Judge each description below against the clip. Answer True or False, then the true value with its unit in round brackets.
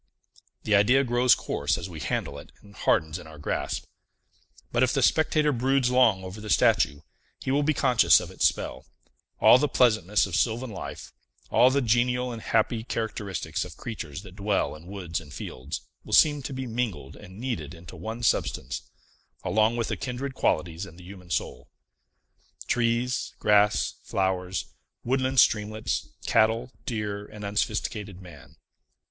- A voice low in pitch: True (110 Hz)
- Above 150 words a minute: True (160 wpm)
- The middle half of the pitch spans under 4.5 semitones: False (4.9 semitones)